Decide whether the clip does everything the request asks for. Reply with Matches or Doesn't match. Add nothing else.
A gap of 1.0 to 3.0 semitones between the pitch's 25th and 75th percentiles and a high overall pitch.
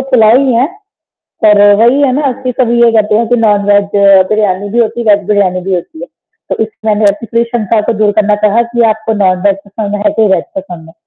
Matches